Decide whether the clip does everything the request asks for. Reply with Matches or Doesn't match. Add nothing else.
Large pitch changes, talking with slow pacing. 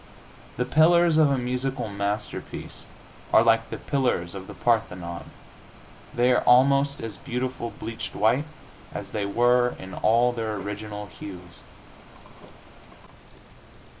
Doesn't match